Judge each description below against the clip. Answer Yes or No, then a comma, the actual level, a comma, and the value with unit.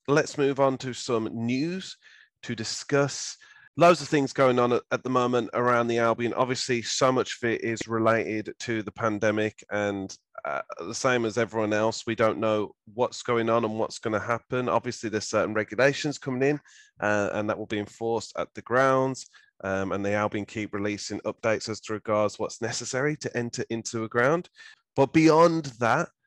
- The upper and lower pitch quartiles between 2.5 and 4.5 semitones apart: Yes, average, 3.3 semitones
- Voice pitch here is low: Yes, low, 115 Hz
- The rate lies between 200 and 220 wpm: No, average, 185 wpm